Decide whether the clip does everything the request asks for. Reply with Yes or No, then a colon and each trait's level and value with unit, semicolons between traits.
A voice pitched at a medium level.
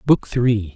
No: low, 110 Hz